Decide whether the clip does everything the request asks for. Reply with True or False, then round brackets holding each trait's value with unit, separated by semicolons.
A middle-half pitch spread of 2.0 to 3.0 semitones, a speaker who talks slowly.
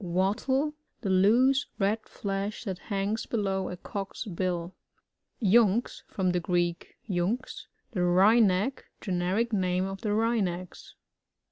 False (3.5 semitones; 130 wpm)